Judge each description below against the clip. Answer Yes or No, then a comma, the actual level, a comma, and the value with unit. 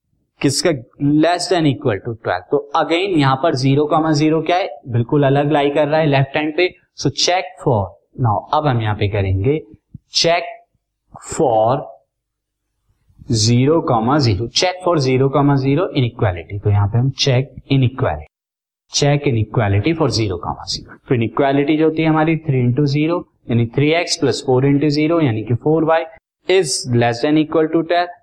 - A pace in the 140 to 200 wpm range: Yes, average, 165 wpm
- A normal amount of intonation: Yes, average, 5.0 semitones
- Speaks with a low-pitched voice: No, medium, 145 Hz